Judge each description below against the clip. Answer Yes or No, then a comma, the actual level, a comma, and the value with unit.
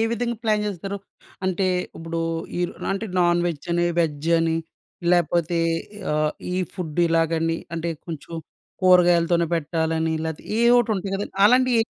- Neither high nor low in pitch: Yes, medium, 170 Hz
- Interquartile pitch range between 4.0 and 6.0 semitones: No, average, 3.1 semitones